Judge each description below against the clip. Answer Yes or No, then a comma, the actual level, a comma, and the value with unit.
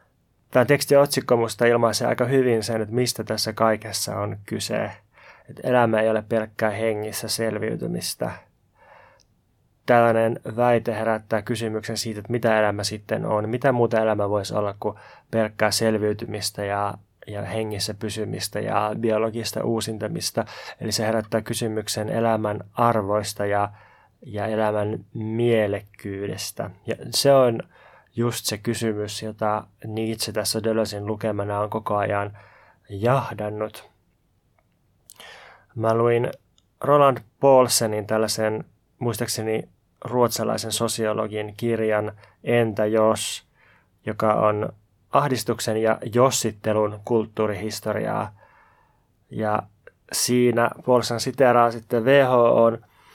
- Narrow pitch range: Yes, narrow, 1.8 semitones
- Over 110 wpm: No, average, 105 wpm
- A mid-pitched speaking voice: No, low, 110 Hz